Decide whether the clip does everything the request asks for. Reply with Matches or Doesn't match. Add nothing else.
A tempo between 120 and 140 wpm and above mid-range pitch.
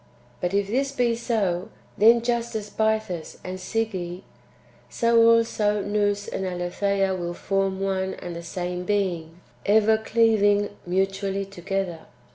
Matches